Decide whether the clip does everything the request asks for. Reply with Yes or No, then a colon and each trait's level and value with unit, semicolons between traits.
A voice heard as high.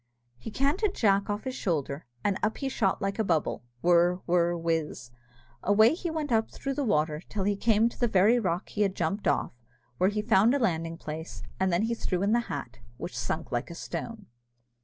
Yes: high, 200 Hz